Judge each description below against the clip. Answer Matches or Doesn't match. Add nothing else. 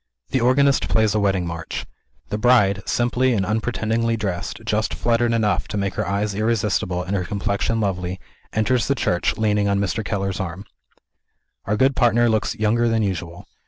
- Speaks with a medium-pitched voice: Doesn't match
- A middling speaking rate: Matches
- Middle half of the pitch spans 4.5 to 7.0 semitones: Doesn't match